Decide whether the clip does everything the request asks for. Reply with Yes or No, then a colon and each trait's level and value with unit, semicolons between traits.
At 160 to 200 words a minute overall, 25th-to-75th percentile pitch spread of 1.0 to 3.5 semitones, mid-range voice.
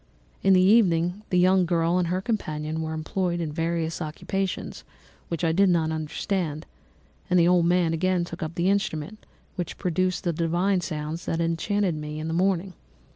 Yes: average, 185 wpm; narrow, 2.4 semitones; medium, 170 Hz